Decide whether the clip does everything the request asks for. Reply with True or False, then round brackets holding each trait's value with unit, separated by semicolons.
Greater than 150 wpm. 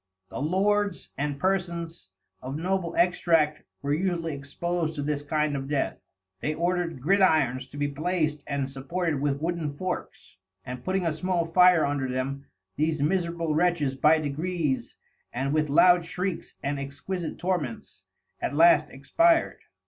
False (145 wpm)